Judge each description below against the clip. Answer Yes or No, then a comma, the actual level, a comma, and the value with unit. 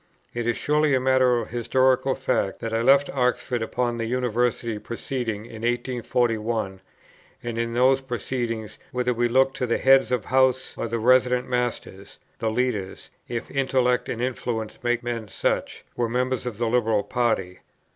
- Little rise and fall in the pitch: Yes, narrow, 1.8 semitones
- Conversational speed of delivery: Yes, average, 165 wpm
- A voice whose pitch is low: Yes, low, 120 Hz